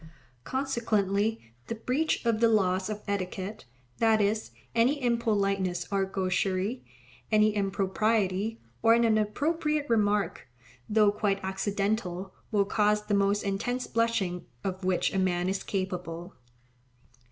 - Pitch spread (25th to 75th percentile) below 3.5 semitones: Yes, average, 2.9 semitones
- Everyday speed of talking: No, slow, 120 wpm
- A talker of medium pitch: No, high, 205 Hz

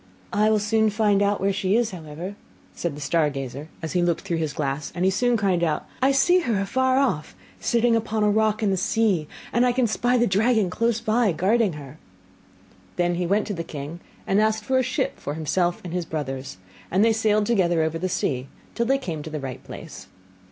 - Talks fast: Yes, fast, 220 wpm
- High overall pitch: Yes, high, 195 Hz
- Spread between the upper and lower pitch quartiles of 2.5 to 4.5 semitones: No, wide, 5.6 semitones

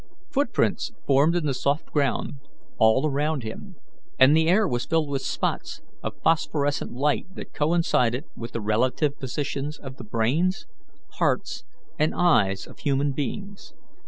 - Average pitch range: Yes, average, 3.8 semitones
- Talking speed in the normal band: Yes, average, 145 wpm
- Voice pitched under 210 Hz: Yes, medium, 140 Hz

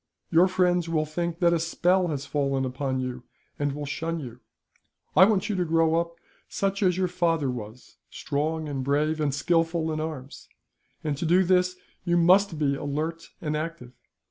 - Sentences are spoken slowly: No, average, 180 wpm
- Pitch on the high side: No, medium, 160 Hz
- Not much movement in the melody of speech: No, average, 3.3 semitones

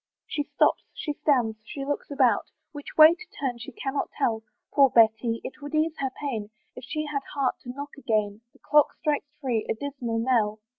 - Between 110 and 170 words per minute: No, average, 195 wpm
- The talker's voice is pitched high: Yes, very high, 270 Hz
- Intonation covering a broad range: No, average, 4.0 semitones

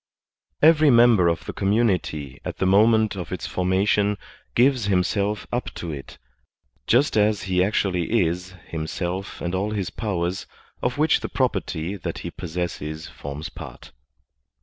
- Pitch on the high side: No, very low, 95 Hz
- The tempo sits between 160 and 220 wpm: No, average, 145 wpm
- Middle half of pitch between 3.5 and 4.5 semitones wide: Yes, average, 3.8 semitones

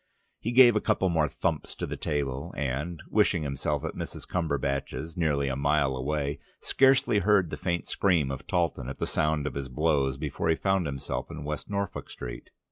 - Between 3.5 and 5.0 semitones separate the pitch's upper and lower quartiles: Yes, average, 4.2 semitones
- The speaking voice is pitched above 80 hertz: No, very low, 75 Hz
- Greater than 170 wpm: Yes, average, 190 wpm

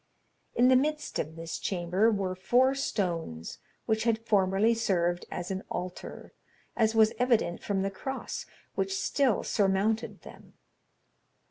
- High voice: Yes, high, 205 Hz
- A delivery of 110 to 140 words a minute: Yes, slow, 135 wpm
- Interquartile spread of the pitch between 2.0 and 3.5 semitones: No, average, 4.1 semitones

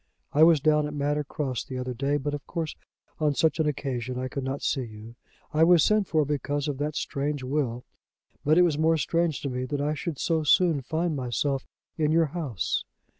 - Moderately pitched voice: Yes, medium, 145 Hz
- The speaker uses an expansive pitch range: No, average, 3.0 semitones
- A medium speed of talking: No, fast, 215 wpm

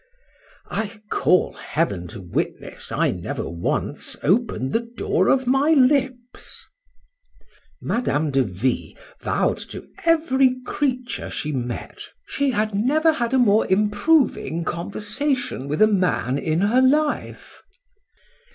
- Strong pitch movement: Yes, wide, 8.7 semitones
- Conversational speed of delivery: No, slow, 115 wpm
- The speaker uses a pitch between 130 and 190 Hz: No, high, 215 Hz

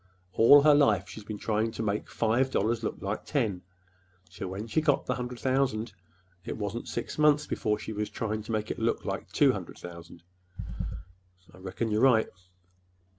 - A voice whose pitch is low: Yes, low, 110 Hz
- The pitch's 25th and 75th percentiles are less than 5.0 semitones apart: Yes, average, 3.2 semitones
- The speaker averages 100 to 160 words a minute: No, average, 180 wpm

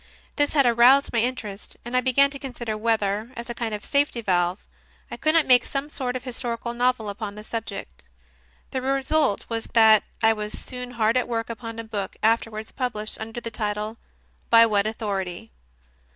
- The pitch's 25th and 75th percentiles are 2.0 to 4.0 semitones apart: Yes, average, 2.8 semitones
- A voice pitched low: No, high, 230 Hz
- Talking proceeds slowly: No, average, 185 wpm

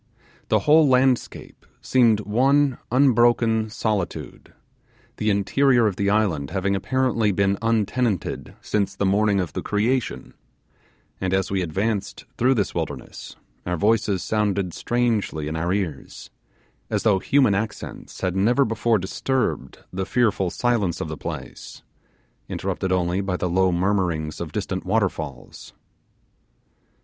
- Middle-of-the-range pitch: No, low, 105 Hz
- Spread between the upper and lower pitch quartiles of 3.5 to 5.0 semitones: Yes, average, 4.0 semitones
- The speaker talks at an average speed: No, slow, 130 wpm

